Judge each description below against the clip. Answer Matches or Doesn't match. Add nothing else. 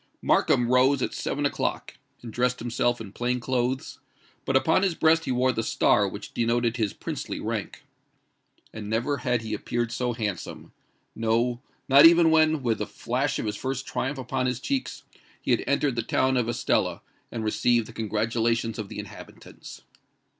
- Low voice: Matches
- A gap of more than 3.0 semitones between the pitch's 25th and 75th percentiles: Doesn't match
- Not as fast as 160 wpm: Doesn't match